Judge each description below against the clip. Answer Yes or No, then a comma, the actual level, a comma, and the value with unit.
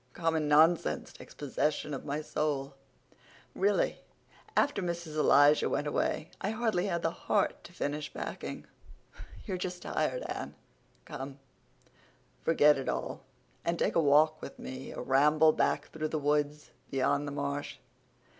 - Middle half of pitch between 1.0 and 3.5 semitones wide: Yes, average, 3.0 semitones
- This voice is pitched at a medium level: Yes, medium, 150 Hz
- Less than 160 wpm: Yes, average, 140 wpm